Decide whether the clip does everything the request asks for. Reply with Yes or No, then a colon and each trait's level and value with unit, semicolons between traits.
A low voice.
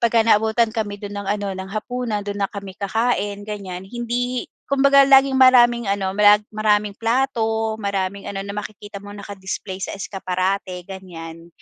No: high, 205 Hz